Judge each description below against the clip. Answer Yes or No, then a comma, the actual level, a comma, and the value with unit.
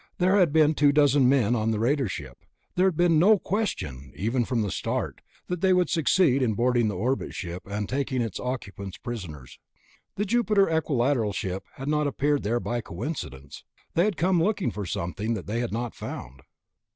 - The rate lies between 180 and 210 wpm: Yes, average, 190 wpm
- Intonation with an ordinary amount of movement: No, wide, 7.3 semitones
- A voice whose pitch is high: No, low, 125 Hz